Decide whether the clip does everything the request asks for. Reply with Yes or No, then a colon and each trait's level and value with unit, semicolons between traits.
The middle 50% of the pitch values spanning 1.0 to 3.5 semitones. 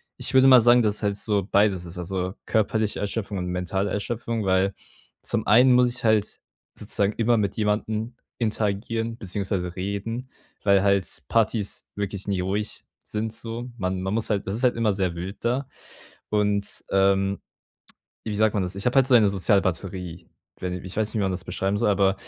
Yes: average, 2.7 semitones